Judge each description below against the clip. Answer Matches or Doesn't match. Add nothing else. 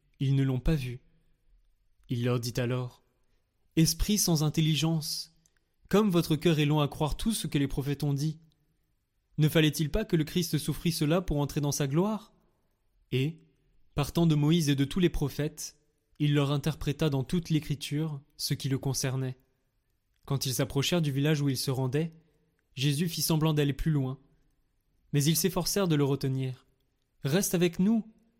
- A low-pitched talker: Doesn't match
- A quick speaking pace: Doesn't match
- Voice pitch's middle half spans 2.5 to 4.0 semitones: Matches